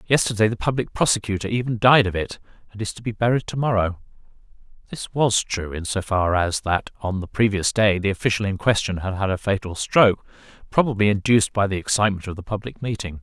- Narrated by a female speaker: No, male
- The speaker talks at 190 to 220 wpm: Yes, average, 200 wpm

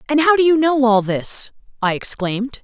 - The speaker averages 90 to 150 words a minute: No, fast, 205 wpm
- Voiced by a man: No, female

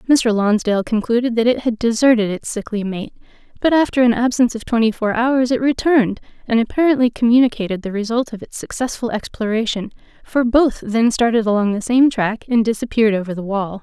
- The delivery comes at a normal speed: Yes, average, 180 wpm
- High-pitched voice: Yes, high, 230 Hz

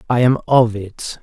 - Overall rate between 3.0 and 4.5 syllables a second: Yes, 3.8 syllables/s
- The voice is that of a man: Yes, male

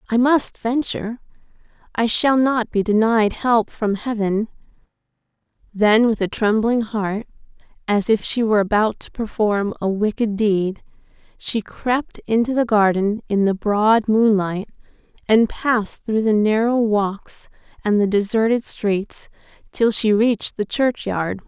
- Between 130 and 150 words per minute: Yes, average, 140 wpm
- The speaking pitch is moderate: No, high, 215 Hz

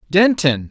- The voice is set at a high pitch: No, medium, 165 Hz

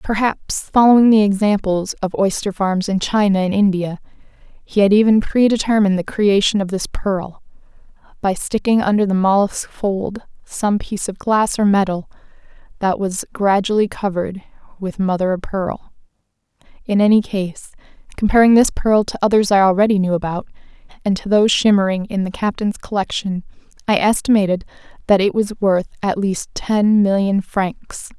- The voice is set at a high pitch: Yes, high, 200 Hz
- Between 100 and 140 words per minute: No, average, 150 wpm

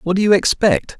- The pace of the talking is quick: Yes, fast, 240 wpm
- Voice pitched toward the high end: No, medium, 180 Hz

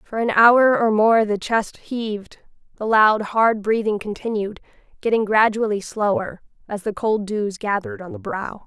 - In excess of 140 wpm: Yes, average, 165 wpm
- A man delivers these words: No, female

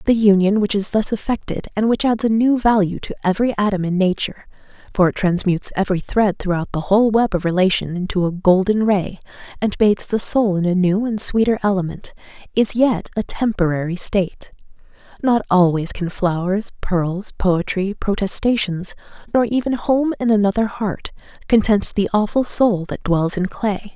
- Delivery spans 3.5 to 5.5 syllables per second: Yes, 5.2 syllables/s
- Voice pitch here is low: No, high, 200 Hz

